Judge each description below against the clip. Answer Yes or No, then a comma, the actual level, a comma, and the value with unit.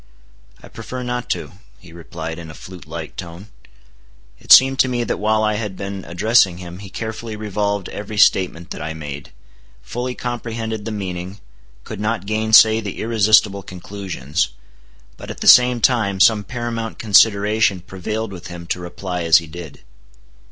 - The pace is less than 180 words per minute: Yes, average, 165 wpm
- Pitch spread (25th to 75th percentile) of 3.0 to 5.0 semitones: Yes, average, 4.1 semitones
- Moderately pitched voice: No, low, 100 Hz